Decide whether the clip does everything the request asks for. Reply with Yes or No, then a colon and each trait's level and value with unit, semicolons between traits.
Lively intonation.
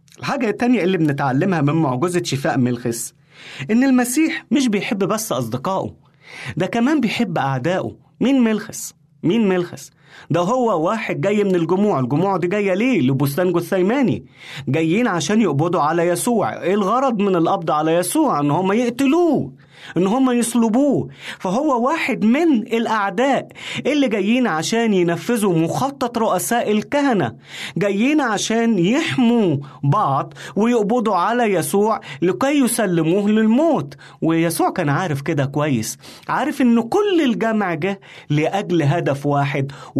Yes: wide, 6.6 semitones